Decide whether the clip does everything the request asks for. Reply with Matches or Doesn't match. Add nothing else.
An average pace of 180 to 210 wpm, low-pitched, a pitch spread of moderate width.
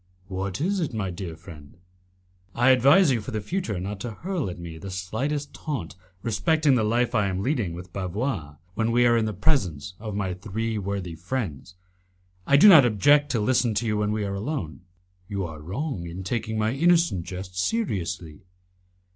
Doesn't match